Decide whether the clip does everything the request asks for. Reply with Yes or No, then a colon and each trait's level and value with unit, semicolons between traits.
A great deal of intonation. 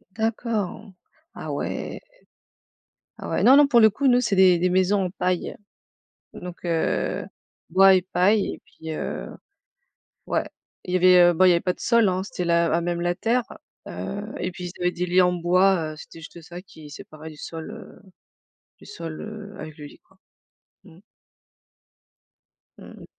No: average, 3.0 semitones